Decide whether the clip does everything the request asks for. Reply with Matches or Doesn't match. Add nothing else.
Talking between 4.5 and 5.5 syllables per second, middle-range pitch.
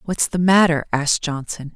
Matches